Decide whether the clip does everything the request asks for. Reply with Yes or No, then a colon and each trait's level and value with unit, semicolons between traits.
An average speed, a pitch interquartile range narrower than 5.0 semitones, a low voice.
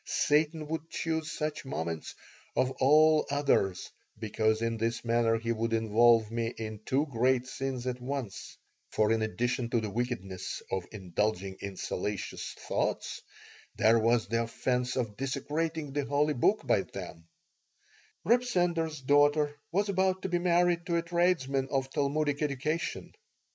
No: average, 150 wpm; average, 5.3 semitones; low, 130 Hz